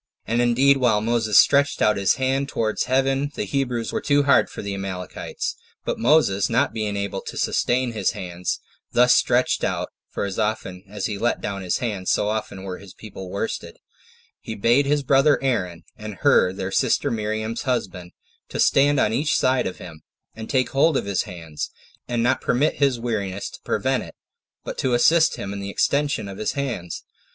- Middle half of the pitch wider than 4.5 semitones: Yes, average, 5.0 semitones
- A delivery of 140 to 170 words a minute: No, average, 195 wpm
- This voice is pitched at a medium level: No, low, 115 Hz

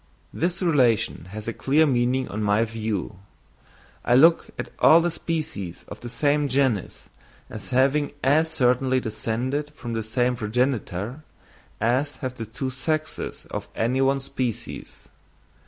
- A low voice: Yes, low, 130 Hz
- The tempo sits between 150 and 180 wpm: No, average, 140 wpm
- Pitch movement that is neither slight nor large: Yes, average, 4.1 semitones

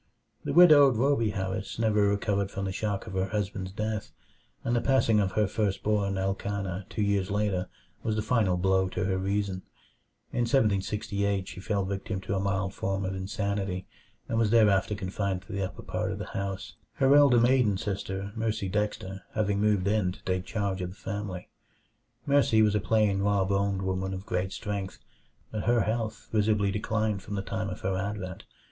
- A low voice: Yes, low, 100 Hz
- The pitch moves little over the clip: Yes, narrow, 2.0 semitones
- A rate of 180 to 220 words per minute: Yes, average, 185 wpm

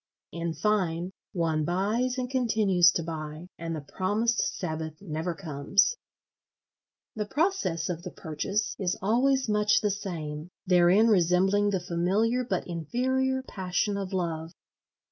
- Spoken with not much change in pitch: No, average, 4.3 semitones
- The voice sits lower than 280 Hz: Yes, medium, 185 Hz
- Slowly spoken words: Yes, slow, 130 wpm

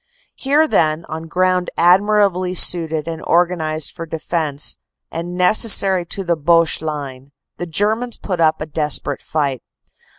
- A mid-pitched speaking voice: Yes, medium, 170 Hz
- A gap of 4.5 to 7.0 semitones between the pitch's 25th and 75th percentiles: No, average, 2.9 semitones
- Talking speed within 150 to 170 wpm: No, slow, 135 wpm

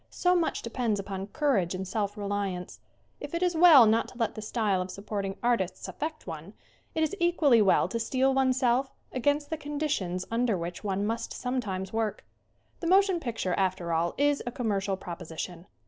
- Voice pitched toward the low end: No, high, 225 Hz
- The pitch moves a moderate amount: No, wide, 6.3 semitones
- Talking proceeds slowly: No, average, 180 wpm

